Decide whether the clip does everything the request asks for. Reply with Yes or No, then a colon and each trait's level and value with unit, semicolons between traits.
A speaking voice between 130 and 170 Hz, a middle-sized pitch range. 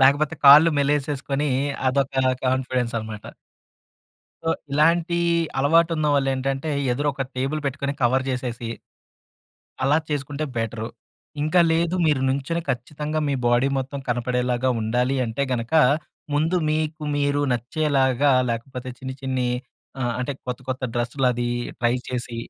Yes: low, 135 Hz; average, 3.0 semitones